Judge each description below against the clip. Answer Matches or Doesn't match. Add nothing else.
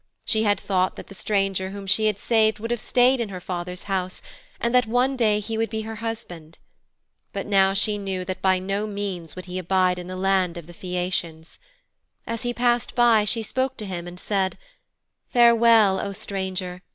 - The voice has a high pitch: Matches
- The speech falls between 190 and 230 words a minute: Matches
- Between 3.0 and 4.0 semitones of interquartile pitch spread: Matches